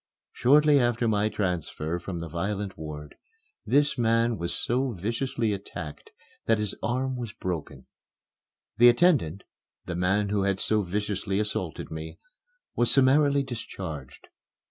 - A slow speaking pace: Yes, slow, 130 wpm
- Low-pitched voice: Yes, low, 105 Hz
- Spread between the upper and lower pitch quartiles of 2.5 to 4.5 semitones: No, average, 5.2 semitones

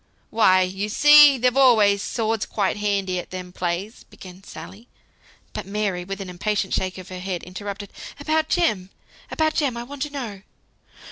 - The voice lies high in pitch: Yes, high, 205 Hz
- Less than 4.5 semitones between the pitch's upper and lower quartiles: No, average, 4.8 semitones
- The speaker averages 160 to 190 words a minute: Yes, average, 165 wpm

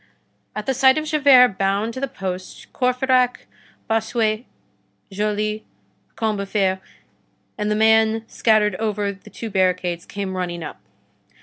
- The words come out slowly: Yes, slow, 125 wpm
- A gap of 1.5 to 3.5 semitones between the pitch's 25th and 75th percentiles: Yes, average, 3.1 semitones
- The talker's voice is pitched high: Yes, high, 215 Hz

